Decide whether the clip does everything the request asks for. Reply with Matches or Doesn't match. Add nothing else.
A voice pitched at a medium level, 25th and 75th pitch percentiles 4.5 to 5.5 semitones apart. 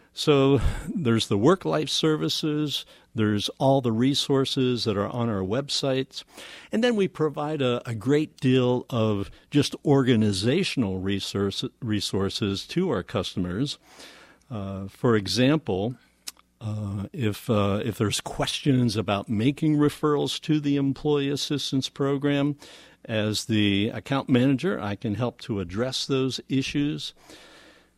Doesn't match